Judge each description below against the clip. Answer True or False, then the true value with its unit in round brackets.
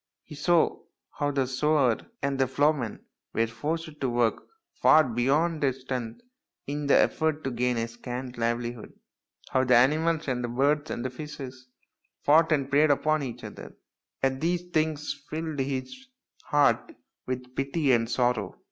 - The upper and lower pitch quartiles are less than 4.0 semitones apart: True (3.5 semitones)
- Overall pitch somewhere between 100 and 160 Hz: True (135 Hz)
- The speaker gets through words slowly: False (150 wpm)